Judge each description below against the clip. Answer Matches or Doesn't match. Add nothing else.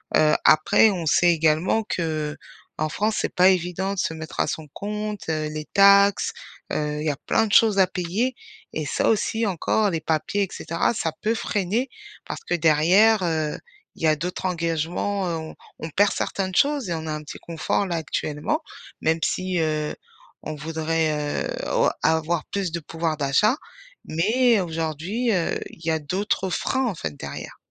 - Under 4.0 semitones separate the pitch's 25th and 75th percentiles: Doesn't match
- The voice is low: Doesn't match